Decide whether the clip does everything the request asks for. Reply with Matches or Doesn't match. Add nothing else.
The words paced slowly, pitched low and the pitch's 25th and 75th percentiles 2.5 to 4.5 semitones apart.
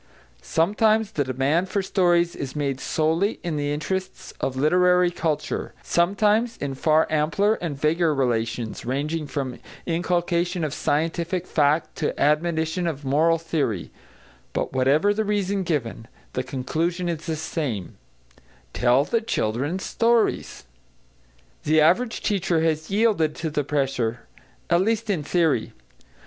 Doesn't match